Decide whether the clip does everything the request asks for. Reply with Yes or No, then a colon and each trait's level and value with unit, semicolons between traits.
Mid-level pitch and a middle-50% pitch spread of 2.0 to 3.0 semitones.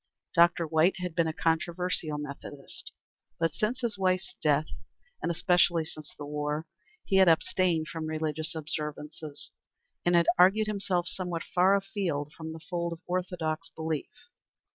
Yes: medium, 165 Hz; narrow, 2.5 semitones